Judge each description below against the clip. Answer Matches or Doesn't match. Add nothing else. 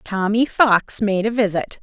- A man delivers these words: Doesn't match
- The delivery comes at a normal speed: Matches